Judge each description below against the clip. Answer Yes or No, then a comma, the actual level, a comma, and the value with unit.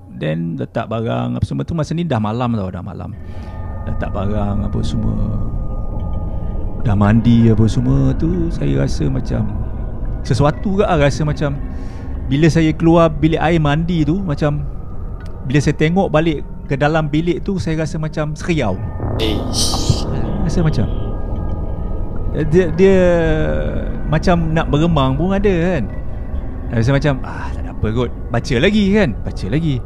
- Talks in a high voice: No, low, 115 Hz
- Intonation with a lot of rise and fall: Yes, wide, 8.7 semitones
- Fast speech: No, average, 145 wpm